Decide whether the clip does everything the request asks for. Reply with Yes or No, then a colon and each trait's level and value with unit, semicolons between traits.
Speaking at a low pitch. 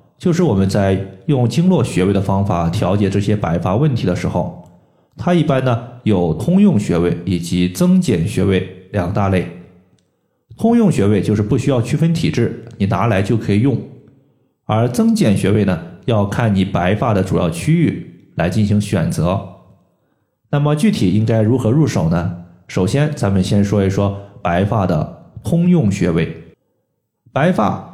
Yes: low, 105 Hz